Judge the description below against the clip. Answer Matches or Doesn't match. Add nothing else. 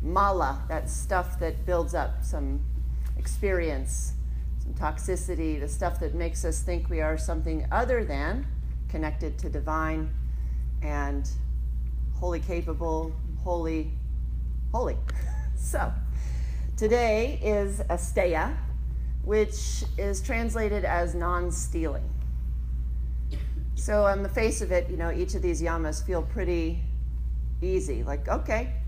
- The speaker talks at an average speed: Doesn't match